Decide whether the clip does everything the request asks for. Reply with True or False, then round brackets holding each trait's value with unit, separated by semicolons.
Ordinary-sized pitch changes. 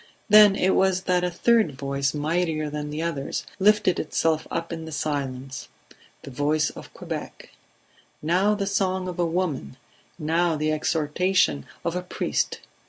True (3.6 semitones)